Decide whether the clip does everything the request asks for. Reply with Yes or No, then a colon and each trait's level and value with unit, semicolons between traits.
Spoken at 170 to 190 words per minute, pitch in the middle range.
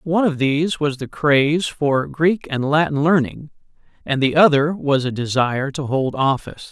Yes: average, 180 wpm; medium, 145 Hz